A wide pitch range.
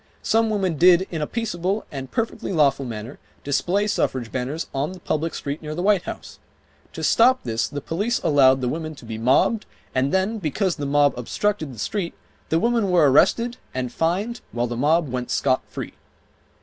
Yes: wide, 6.8 semitones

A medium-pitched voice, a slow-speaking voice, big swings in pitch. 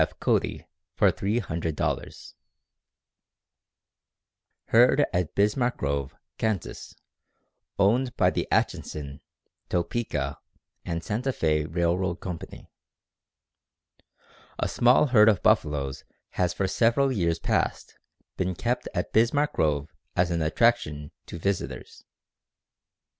No: very low, 90 Hz; slow, 100 wpm; wide, 6.8 semitones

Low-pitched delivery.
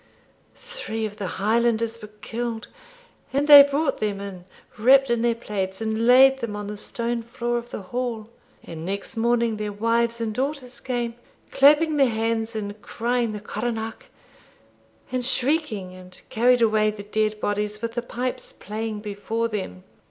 No: high, 230 Hz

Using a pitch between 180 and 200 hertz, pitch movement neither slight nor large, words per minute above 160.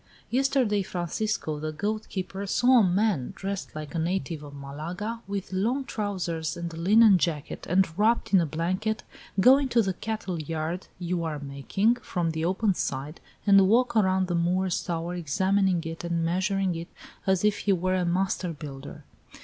Yes: medium, 185 Hz; average, 3.6 semitones; average, 175 wpm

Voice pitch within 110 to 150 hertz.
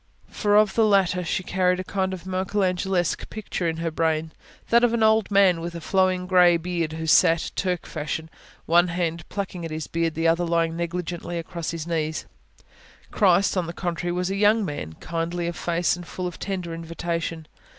No: medium, 175 Hz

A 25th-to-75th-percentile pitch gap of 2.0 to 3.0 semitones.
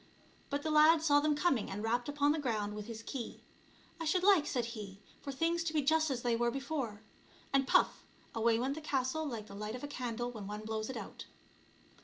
No: average, 5.1 semitones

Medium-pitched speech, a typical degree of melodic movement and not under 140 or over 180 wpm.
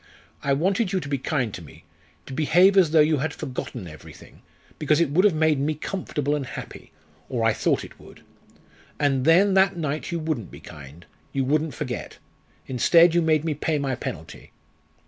No: medium, 150 Hz; average, 3.8 semitones; average, 190 wpm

